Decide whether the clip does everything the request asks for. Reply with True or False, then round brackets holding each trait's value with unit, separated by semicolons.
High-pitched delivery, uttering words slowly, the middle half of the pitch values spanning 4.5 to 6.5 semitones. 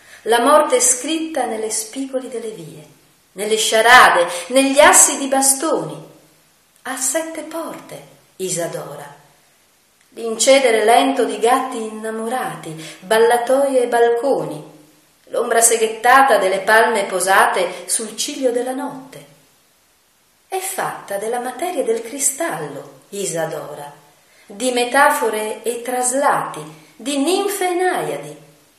True (235 Hz; 100 wpm; 5.5 semitones)